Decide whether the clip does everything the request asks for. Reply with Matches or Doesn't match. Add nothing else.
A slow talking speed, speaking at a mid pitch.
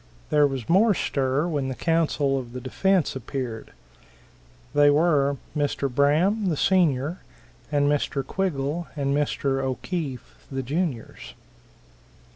Matches